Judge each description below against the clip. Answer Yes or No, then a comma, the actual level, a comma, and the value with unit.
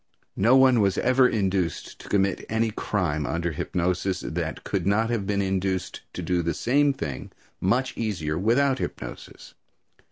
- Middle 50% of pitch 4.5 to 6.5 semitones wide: Yes, average, 4.8 semitones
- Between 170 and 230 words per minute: No, average, 155 wpm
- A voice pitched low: Yes, low, 100 Hz